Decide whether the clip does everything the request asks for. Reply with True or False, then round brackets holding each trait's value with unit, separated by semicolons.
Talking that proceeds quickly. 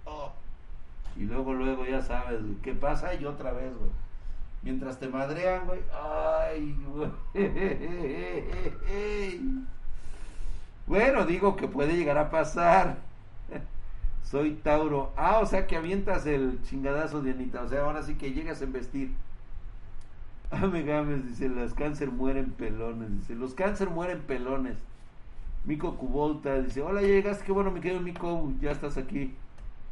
False (140 wpm)